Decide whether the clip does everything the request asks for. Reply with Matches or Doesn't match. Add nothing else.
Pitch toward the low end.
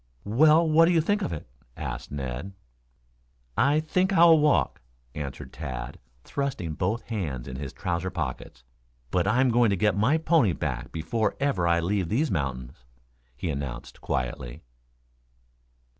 Matches